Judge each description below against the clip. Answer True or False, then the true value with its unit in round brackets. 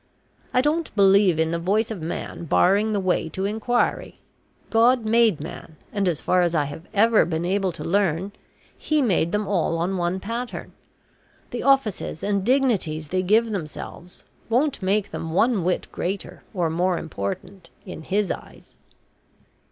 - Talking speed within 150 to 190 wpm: True (160 wpm)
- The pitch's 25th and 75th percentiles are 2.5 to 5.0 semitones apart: True (4.3 semitones)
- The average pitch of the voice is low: False (195 Hz)